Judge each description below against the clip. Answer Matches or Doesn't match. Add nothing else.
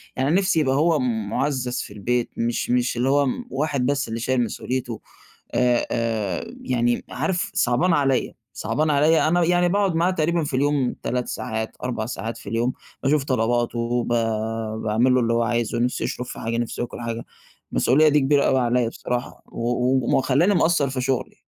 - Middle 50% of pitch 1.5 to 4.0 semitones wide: Matches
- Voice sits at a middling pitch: Doesn't match